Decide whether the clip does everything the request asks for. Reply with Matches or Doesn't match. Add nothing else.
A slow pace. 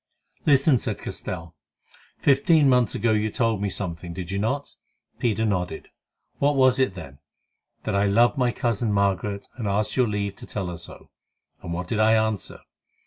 Doesn't match